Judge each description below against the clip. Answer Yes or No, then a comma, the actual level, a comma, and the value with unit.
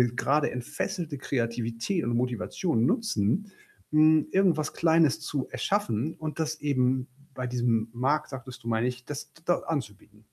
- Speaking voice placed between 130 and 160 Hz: Yes, low, 135 Hz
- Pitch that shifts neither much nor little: Yes, average, 4.9 semitones